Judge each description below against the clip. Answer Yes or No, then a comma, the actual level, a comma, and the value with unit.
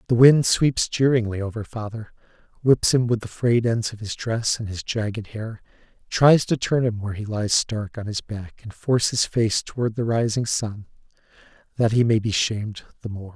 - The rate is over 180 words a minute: Yes, average, 200 wpm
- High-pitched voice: No, low, 110 Hz